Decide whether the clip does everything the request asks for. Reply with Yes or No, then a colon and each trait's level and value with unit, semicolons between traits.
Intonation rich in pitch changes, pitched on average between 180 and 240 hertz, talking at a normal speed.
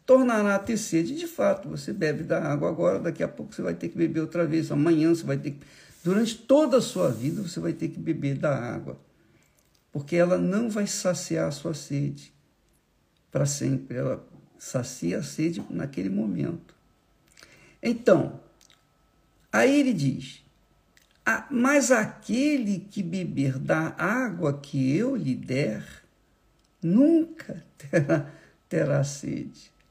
No: wide, 7.0 semitones; medium, 170 Hz; average, 145 wpm